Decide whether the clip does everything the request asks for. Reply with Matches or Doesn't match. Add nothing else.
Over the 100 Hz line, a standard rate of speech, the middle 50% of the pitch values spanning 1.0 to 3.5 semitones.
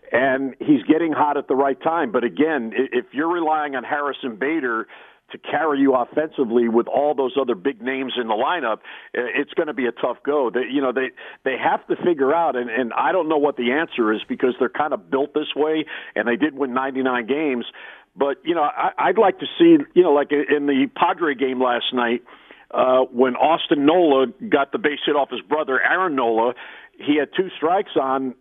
Doesn't match